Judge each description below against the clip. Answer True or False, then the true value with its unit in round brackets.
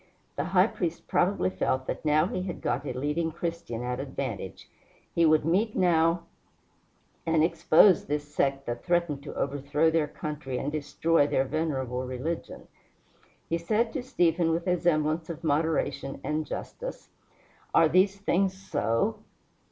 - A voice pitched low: False (155 Hz)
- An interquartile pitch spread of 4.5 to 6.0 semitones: False (3.4 semitones)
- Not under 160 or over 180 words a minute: False (150 wpm)